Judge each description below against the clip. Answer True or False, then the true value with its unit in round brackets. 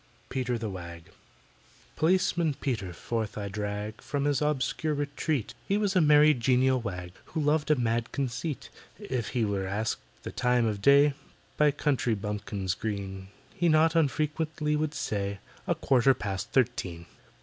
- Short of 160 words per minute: True (150 wpm)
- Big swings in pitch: True (6.4 semitones)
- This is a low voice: True (125 Hz)